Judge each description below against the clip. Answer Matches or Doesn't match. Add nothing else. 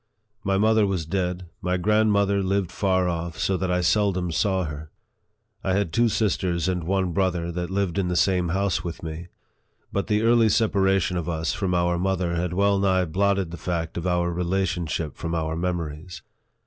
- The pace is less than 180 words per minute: Doesn't match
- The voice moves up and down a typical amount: Doesn't match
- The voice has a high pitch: Doesn't match